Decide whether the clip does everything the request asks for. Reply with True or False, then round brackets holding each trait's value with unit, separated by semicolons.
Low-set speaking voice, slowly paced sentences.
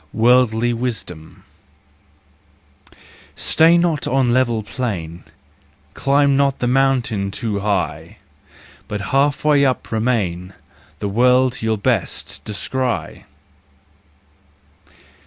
True (120 Hz; 90 wpm)